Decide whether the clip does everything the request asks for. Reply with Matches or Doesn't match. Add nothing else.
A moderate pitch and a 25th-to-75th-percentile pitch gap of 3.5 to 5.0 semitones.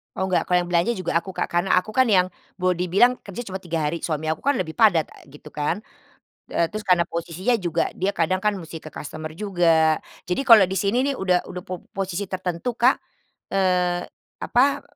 Doesn't match